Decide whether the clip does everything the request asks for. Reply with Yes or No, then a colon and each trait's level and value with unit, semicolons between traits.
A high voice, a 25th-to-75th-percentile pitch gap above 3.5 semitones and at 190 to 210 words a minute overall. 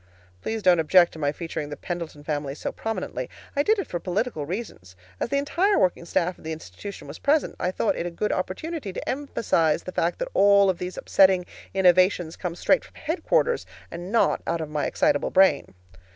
No: medium, 180 Hz; average, 5.3 semitones; average, 200 wpm